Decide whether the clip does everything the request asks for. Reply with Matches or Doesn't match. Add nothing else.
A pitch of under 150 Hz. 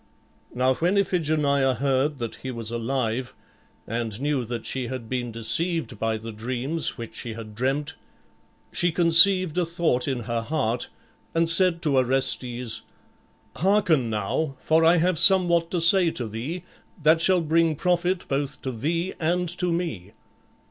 Matches